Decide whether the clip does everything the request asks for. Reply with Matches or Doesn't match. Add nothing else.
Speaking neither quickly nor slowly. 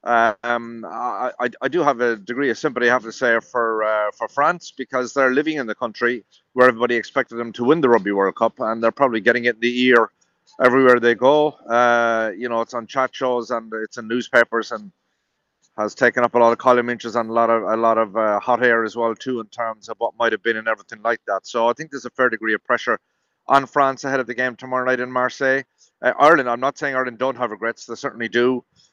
Doesn't match